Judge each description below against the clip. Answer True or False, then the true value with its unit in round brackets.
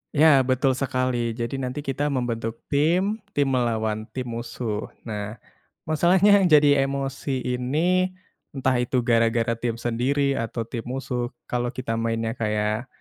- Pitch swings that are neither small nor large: True (3.4 semitones)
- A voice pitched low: True (125 Hz)